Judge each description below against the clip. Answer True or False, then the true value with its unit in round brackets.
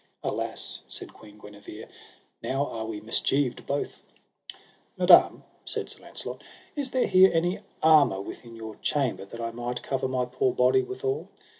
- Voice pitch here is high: False (130 Hz)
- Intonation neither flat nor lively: False (8.4 semitones)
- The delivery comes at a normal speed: True (150 wpm)